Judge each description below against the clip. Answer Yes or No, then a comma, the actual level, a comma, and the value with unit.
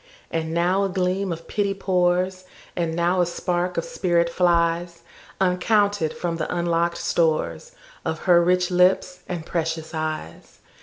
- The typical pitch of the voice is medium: Yes, medium, 175 Hz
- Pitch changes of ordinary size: No, narrow, 1.6 semitones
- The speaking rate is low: Yes, slow, 130 wpm